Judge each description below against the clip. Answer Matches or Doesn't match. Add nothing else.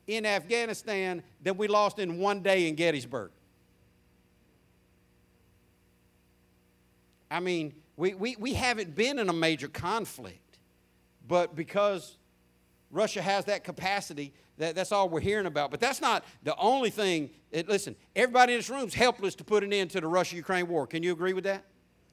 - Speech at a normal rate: Matches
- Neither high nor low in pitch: Matches